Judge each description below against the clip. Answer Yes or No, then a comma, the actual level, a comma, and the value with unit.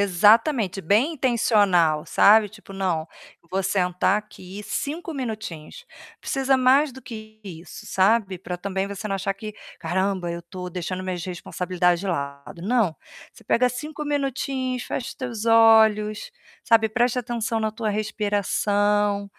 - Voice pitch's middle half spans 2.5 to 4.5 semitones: Yes, average, 4.1 semitones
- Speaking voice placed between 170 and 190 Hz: No, high, 210 Hz